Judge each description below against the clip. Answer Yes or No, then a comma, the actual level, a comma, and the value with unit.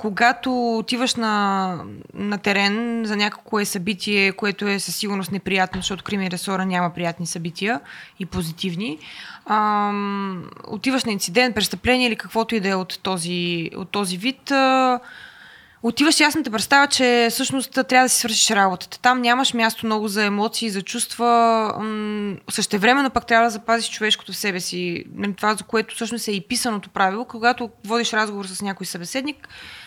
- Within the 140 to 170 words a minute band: Yes, fast, 165 wpm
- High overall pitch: Yes, high, 215 Hz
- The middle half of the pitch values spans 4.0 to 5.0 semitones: No, average, 3.4 semitones